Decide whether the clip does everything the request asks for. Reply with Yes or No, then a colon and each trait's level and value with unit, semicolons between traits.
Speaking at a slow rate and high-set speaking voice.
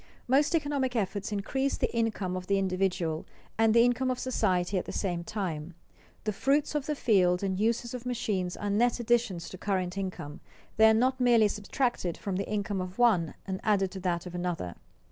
No: average, 200 wpm; high, 205 Hz